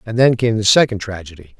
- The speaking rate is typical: No, fast, 225 wpm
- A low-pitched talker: Yes, low, 110 Hz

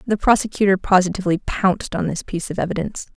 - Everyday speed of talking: Yes, average, 170 wpm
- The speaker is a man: No, female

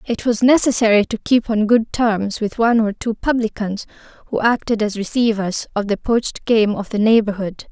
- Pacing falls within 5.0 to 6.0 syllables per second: Yes, 5.1 syllables/s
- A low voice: No, high, 220 Hz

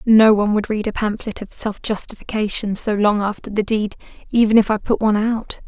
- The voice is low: No, high, 210 Hz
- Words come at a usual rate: No, fast, 210 wpm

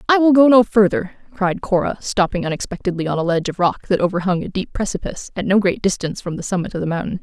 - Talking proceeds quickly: Yes, fast, 240 wpm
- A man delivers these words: No, female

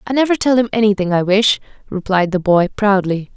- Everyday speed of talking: Yes, average, 195 wpm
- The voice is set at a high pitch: Yes, high, 205 Hz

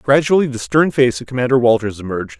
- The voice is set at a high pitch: No, low, 125 Hz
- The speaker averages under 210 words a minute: Yes, average, 200 wpm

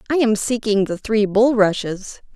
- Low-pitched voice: No, high, 215 Hz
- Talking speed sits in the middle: Yes, average, 155 wpm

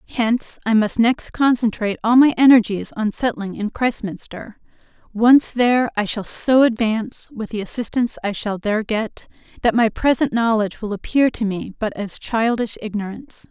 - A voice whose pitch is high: Yes, high, 225 Hz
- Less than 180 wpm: Yes, average, 165 wpm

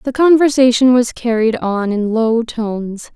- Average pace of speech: Yes, average, 150 wpm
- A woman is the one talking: Yes, female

